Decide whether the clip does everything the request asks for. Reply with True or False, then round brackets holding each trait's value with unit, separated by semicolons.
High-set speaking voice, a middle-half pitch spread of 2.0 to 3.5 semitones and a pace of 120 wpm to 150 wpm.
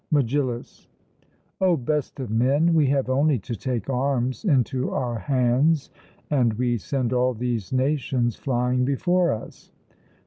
False (130 Hz; 2.8 semitones; 135 wpm)